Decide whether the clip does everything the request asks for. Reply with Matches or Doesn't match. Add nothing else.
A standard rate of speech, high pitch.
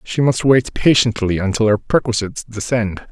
Doesn't match